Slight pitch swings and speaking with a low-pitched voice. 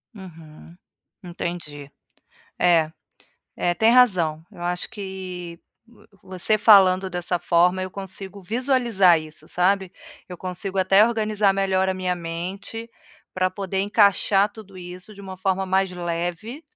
No: narrow, 2.2 semitones; medium, 185 Hz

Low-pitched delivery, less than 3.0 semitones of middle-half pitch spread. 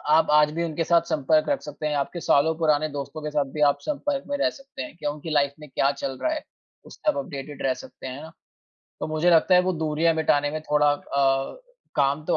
No: medium, 155 Hz; narrow, 2.4 semitones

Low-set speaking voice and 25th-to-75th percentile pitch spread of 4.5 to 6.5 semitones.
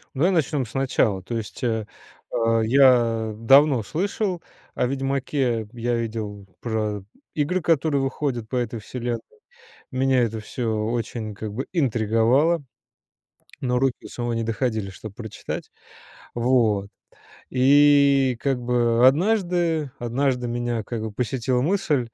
No: low, 125 Hz; average, 3.5 semitones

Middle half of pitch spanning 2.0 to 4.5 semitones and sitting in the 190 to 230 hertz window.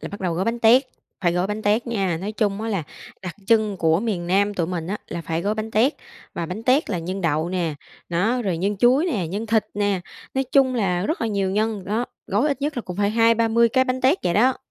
Yes: average, 4.1 semitones; high, 205 Hz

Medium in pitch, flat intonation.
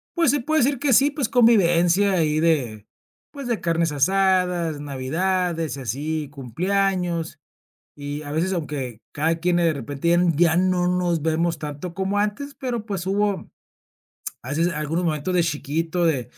No: medium, 170 Hz; average, 4.2 semitones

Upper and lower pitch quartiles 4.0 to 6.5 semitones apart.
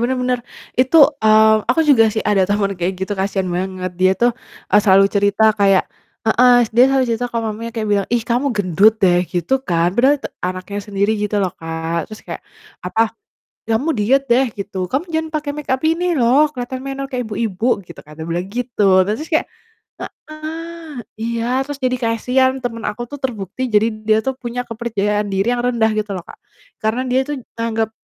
Yes: average, 4.3 semitones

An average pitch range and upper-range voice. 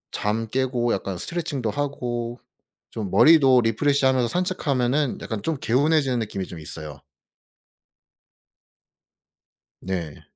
No: average, 4.7 semitones; low, 125 Hz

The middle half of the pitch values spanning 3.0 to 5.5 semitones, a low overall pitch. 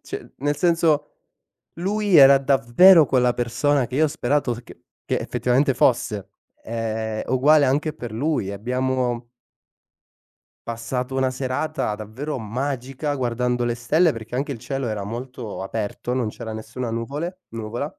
Yes: average, 3.8 semitones; low, 125 Hz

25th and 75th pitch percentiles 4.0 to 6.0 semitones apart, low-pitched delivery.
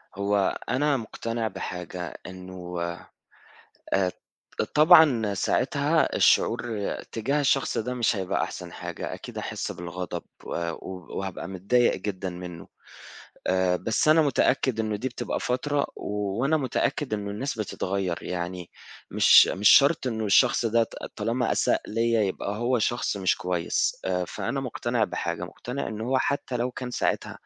Yes: average, 5.1 semitones; low, 110 Hz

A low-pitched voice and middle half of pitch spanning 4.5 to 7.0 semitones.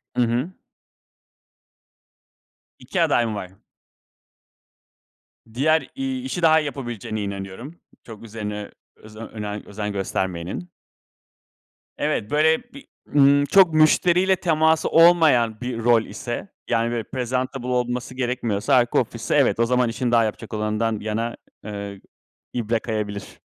Yes: low, 120 Hz; average, 5.1 semitones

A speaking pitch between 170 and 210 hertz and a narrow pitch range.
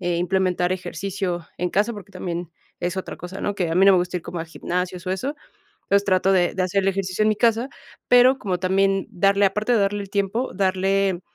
Yes: high, 190 Hz; narrow, 1.9 semitones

